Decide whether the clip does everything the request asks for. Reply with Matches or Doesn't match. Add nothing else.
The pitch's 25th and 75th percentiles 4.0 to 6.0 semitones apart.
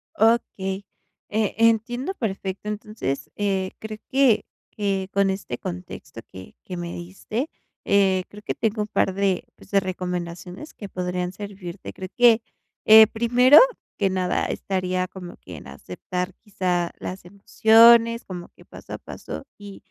Doesn't match